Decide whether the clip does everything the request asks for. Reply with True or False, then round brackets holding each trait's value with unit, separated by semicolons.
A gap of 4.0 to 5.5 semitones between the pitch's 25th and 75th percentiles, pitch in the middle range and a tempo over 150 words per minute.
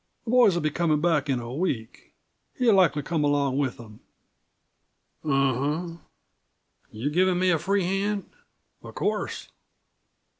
False (5.1 semitones; 155 Hz; 140 wpm)